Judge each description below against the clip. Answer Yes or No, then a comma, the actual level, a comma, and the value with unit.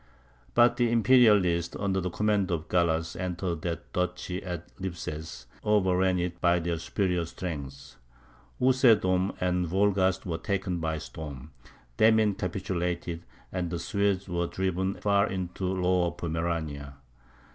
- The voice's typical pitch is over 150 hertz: No, very low, 90 Hz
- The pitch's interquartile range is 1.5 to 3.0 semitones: Yes, narrow, 2.4 semitones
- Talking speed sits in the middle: No, slow, 130 wpm